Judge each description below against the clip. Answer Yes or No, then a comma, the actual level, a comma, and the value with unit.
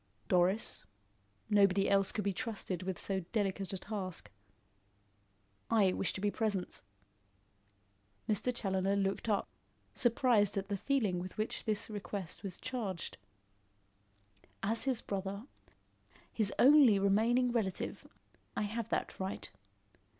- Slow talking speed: Yes, slow, 120 wpm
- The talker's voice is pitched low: No, high, 200 Hz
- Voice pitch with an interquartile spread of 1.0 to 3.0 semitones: Yes, narrow, 2.6 semitones